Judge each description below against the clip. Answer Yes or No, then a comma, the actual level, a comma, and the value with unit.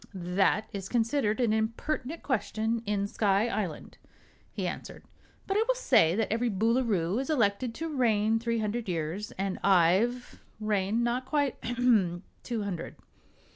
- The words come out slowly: No, average, 145 wpm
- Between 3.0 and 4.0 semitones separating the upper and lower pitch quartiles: Yes, average, 3.6 semitones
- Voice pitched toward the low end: No, high, 220 Hz